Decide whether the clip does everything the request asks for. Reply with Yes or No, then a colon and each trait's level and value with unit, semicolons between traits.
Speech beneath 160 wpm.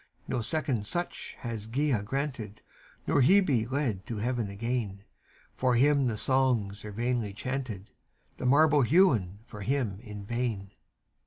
Yes: average, 140 wpm